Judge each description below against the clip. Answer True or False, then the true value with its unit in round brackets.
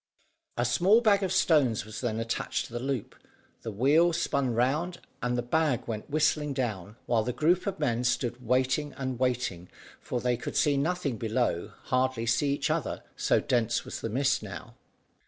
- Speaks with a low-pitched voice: True (130 Hz)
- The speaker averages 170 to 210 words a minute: True (180 wpm)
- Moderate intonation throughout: True (4.0 semitones)